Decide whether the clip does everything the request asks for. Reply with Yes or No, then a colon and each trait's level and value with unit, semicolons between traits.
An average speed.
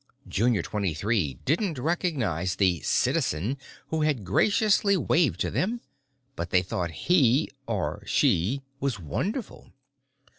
No: slow, 110 wpm